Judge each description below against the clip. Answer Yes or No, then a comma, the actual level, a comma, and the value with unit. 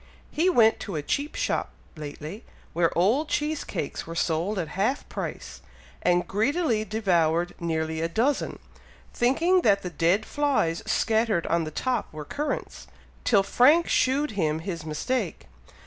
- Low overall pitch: No, high, 200 Hz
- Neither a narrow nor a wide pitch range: No, wide, 7.7 semitones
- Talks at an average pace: Yes, average, 150 wpm